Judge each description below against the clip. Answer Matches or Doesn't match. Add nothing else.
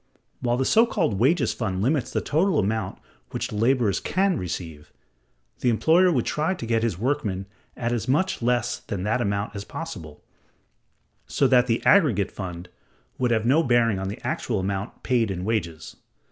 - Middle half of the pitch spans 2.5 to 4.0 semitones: Doesn't match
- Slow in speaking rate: Doesn't match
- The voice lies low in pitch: Matches